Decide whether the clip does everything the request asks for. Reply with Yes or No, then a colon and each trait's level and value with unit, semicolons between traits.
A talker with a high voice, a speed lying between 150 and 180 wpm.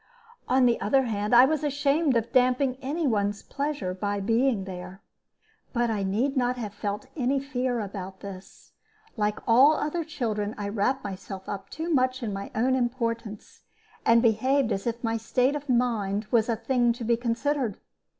Yes: high, 235 Hz; average, 175 wpm